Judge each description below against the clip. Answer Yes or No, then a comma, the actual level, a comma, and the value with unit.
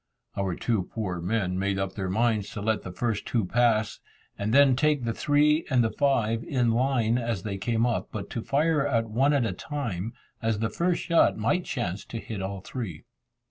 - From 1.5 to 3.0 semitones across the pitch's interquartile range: No, average, 4.4 semitones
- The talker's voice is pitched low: Yes, low, 115 Hz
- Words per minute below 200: No, fast, 205 wpm